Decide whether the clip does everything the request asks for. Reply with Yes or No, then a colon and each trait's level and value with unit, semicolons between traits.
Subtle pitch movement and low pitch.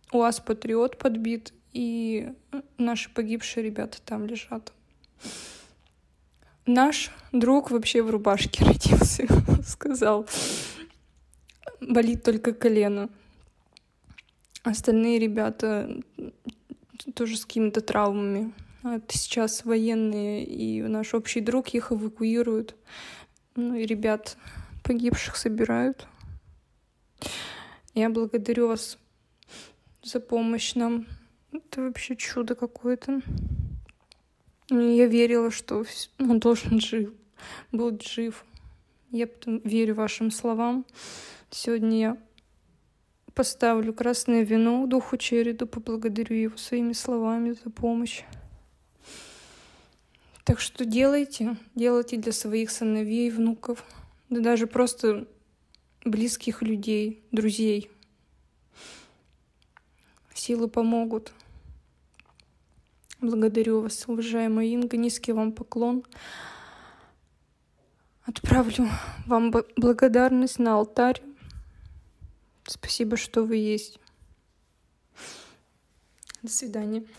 No: narrow, 1.6 semitones; high, 230 Hz